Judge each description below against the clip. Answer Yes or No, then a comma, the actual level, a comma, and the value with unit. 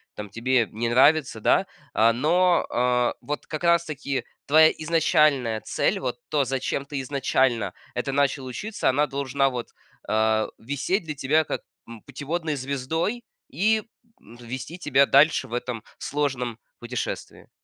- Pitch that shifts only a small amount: No, average, 3.9 semitones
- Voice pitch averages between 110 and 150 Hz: Yes, low, 135 Hz